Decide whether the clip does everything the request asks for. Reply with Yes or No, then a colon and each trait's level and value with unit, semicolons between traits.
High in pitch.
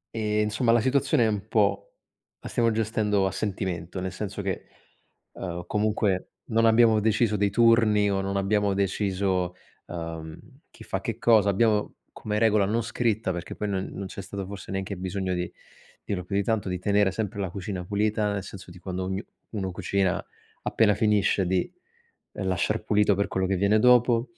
No: low, 100 Hz